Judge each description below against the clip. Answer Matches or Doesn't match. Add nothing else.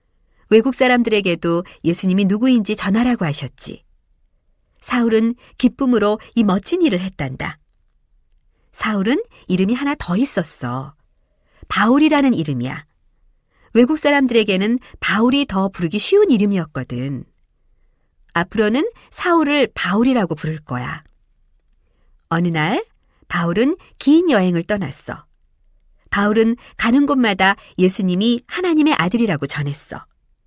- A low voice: Doesn't match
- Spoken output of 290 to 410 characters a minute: Doesn't match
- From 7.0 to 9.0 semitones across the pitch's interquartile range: Matches